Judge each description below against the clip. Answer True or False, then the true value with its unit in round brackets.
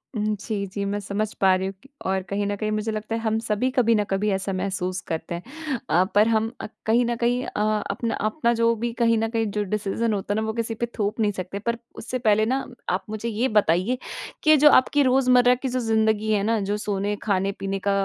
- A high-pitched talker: True (215 Hz)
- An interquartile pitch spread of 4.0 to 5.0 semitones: False (2.7 semitones)